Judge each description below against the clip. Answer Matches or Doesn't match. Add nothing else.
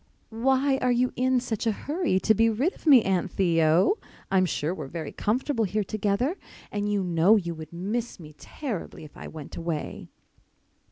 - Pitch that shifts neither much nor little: Doesn't match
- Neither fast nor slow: Matches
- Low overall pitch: Doesn't match